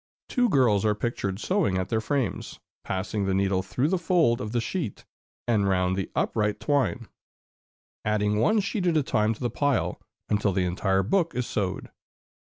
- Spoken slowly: No, average, 180 wpm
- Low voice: Yes, low, 110 Hz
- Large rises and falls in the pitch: Yes, wide, 6.5 semitones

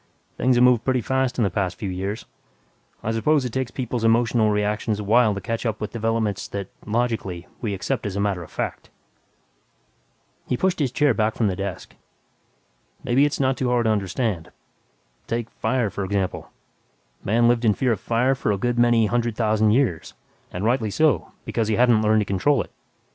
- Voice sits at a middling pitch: No, low, 115 Hz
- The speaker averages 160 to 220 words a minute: Yes, average, 190 wpm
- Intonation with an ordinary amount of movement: Yes, average, 3.1 semitones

